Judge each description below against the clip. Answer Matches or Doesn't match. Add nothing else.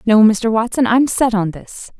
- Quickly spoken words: Matches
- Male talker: Doesn't match